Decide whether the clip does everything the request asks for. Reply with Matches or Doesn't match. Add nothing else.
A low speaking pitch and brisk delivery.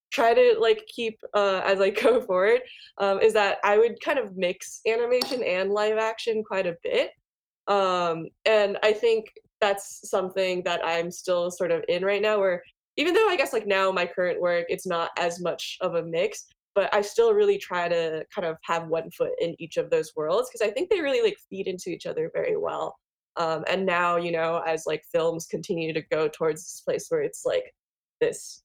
Doesn't match